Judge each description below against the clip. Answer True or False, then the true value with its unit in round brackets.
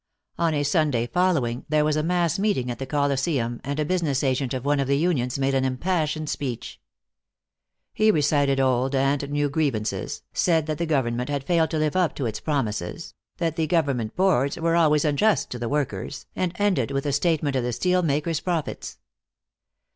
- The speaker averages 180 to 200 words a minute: True (190 wpm)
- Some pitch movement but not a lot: True (3.6 semitones)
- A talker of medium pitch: True (145 Hz)